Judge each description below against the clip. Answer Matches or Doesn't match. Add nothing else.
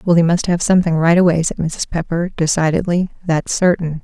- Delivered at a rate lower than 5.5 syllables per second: Doesn't match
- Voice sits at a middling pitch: Matches